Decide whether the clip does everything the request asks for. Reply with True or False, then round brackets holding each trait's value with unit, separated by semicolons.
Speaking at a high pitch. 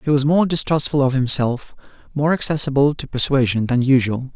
False (140 Hz)